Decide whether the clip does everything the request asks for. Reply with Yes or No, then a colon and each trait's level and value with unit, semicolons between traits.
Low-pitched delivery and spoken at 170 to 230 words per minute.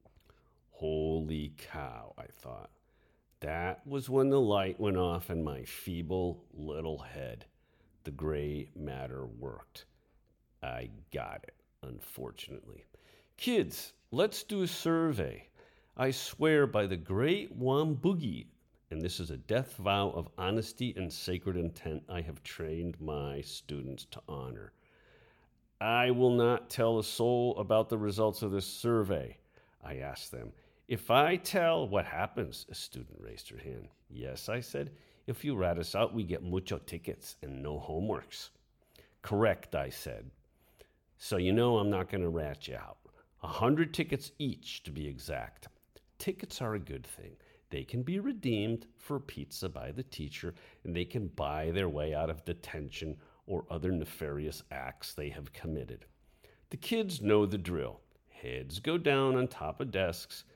No: very low, 95 Hz; average, 155 wpm